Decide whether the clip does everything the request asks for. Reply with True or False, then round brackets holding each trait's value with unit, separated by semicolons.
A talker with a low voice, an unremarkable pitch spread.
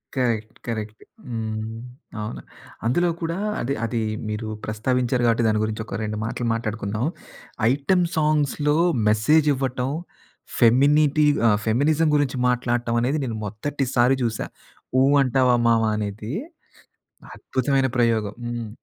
True (120 Hz; 3.8 semitones)